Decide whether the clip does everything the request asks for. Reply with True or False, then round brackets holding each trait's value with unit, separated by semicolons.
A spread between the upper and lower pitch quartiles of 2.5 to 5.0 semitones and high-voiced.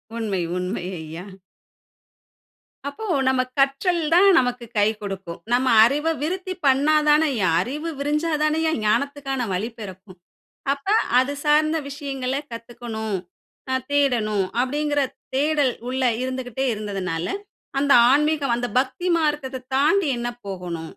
False (5.6 semitones; 265 Hz)